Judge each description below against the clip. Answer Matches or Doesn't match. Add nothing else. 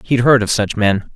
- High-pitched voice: Doesn't match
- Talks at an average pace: Doesn't match